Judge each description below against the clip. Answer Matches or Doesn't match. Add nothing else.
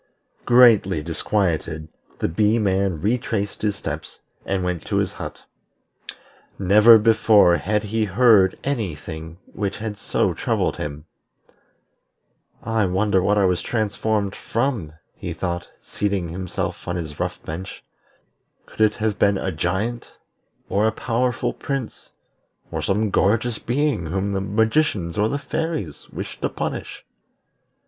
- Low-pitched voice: Matches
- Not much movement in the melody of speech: Doesn't match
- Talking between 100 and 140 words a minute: Matches